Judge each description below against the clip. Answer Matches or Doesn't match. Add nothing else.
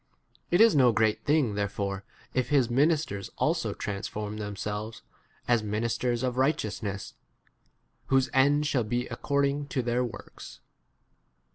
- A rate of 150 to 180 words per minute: Doesn't match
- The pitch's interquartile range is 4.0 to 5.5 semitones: Matches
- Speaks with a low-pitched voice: Matches